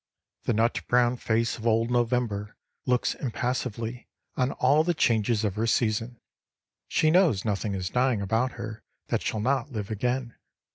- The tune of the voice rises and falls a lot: No, narrow, 2.5 semitones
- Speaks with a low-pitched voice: Yes, low, 115 Hz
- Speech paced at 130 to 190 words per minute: Yes, average, 155 wpm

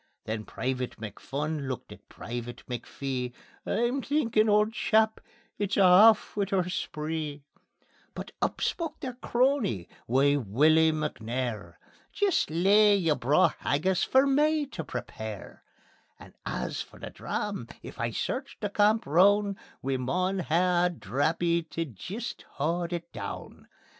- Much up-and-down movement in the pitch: Yes, wide, 7.8 semitones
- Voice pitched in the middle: Yes, medium, 170 Hz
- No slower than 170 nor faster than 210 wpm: No, average, 140 wpm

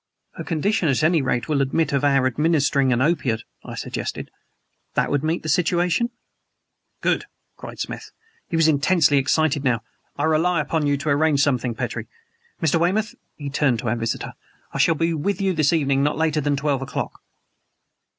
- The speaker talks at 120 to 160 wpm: No, average, 180 wpm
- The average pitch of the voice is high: No, medium, 150 Hz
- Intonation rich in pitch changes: No, average, 3.2 semitones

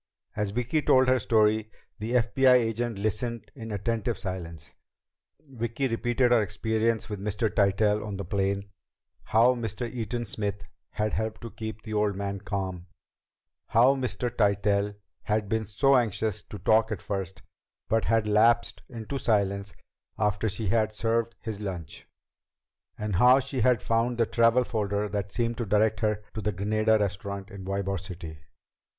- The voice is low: Yes, low, 110 Hz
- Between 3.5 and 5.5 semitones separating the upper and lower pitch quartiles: No, narrow, 2.6 semitones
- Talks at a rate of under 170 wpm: Yes, average, 155 wpm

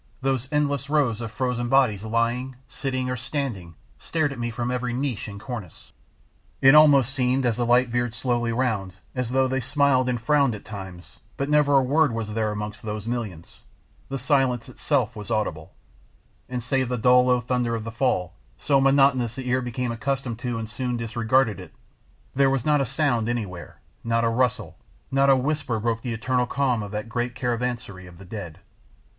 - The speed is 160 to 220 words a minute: Yes, average, 190 wpm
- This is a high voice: No, low, 125 Hz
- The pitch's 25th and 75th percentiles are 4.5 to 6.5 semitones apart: No, average, 2.9 semitones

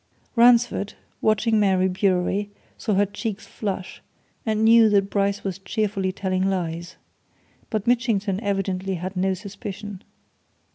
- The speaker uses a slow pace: Yes, slow, 125 wpm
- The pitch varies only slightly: Yes, narrow, 2.2 semitones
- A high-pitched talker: Yes, high, 200 Hz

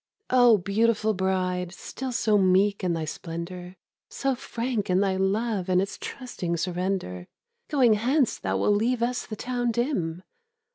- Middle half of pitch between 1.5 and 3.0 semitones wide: No, average, 4.6 semitones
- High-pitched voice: Yes, high, 200 Hz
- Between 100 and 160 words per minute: Yes, average, 150 wpm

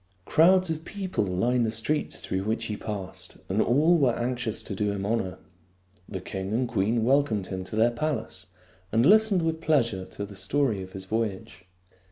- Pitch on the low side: Yes, low, 115 Hz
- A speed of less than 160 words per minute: No, average, 185 wpm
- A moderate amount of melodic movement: No, wide, 6.7 semitones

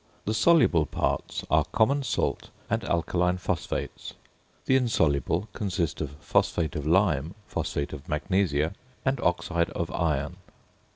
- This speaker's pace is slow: Yes, slow, 125 wpm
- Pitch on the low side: Yes, very low, 85 Hz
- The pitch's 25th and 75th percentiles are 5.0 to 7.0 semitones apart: Yes, wide, 5.4 semitones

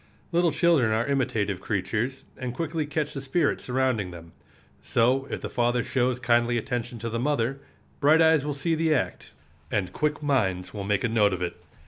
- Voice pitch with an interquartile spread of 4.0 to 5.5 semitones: Yes, average, 4.8 semitones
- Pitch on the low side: Yes, low, 125 Hz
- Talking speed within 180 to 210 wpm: Yes, average, 185 wpm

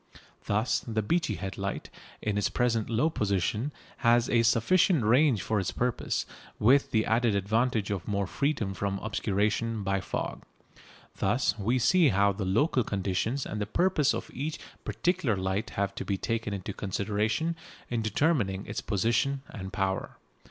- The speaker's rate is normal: Yes, average, 160 wpm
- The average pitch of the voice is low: Yes, low, 110 Hz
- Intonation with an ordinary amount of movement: Yes, average, 3.9 semitones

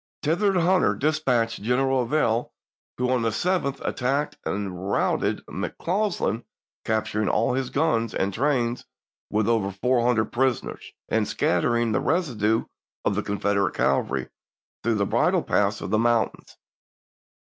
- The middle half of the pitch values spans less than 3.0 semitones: No, average, 4.1 semitones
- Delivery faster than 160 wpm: No, average, 140 wpm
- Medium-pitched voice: No, low, 120 Hz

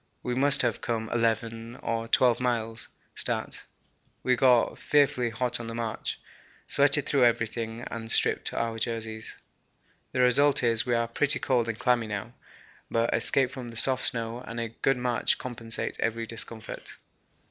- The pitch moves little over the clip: Yes, narrow, 1.6 semitones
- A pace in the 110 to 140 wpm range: No, average, 160 wpm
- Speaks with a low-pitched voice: Yes, low, 115 Hz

